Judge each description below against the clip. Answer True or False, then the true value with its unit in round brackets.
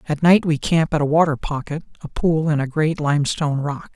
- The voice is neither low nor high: True (155 Hz)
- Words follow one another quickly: True (230 wpm)